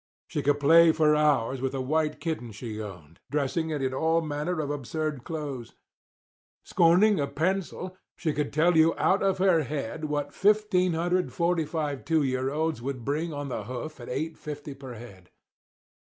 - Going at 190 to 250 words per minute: No, average, 165 wpm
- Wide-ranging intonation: No, average, 3.6 semitones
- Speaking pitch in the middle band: Yes, medium, 150 Hz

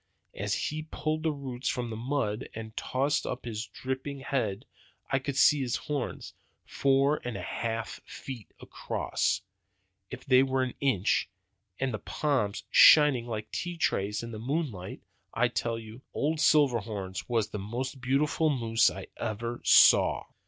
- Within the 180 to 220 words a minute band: No, average, 155 wpm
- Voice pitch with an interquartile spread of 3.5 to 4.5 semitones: Yes, average, 4.0 semitones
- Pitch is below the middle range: Yes, low, 125 Hz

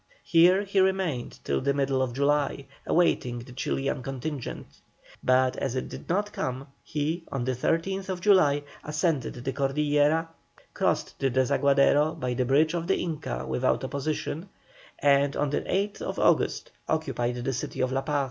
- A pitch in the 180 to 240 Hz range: No, medium, 140 Hz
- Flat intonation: No, average, 3.9 semitones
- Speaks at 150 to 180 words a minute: Yes, average, 155 wpm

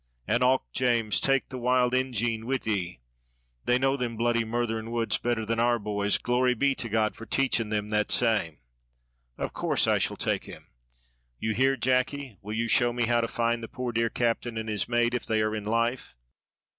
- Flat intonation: Yes, narrow, 2.0 semitones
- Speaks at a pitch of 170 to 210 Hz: No, low, 115 Hz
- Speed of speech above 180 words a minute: Yes, average, 200 wpm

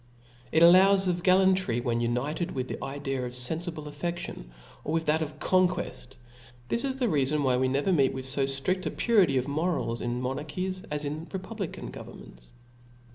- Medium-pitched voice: Yes, medium, 150 Hz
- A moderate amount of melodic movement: No, wide, 5.9 semitones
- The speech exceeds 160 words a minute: Yes, average, 180 wpm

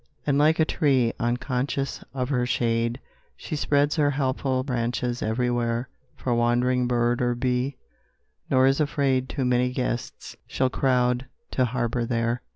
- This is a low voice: Yes, low, 125 Hz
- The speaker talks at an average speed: Yes, average, 145 wpm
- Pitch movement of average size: No, narrow, 1.8 semitones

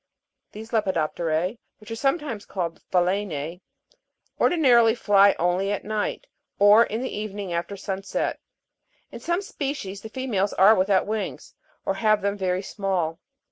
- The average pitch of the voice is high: Yes, high, 200 Hz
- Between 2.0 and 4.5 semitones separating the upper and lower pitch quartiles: Yes, average, 3.0 semitones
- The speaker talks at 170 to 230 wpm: No, average, 140 wpm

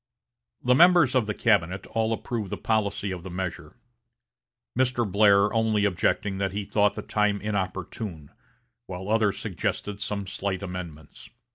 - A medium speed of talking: Yes, average, 145 wpm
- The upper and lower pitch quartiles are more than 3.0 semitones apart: No, average, 2.7 semitones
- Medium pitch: No, low, 100 Hz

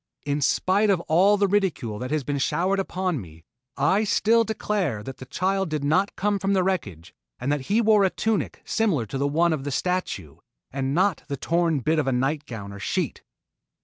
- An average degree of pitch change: No, wide, 6.3 semitones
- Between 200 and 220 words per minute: Yes, fast, 205 wpm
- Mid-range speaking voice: Yes, medium, 160 Hz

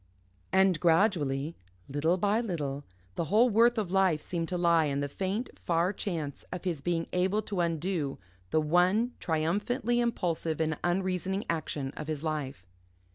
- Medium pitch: Yes, medium, 175 Hz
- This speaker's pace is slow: No, average, 155 wpm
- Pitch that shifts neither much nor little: Yes, average, 3.7 semitones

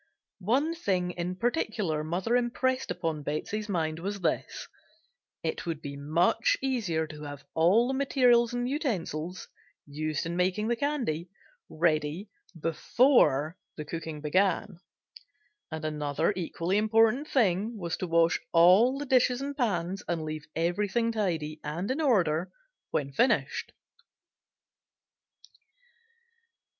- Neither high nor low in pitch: Yes, medium, 180 Hz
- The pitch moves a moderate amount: No, wide, 6.8 semitones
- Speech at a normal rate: No, slow, 125 wpm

